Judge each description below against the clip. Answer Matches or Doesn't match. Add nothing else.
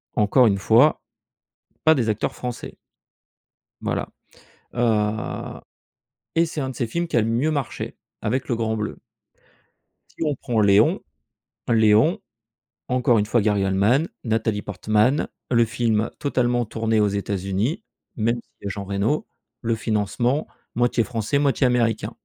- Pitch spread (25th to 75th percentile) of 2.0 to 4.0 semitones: Matches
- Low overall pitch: Matches